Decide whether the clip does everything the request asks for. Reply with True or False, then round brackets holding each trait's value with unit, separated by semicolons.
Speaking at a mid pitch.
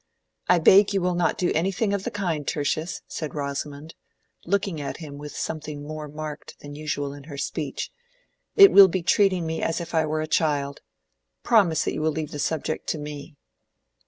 True (155 Hz)